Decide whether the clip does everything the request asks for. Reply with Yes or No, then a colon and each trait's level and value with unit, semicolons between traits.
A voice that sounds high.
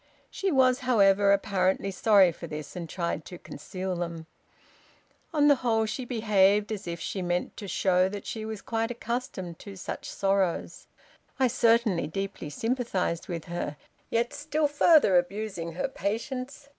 Yes: high, 200 Hz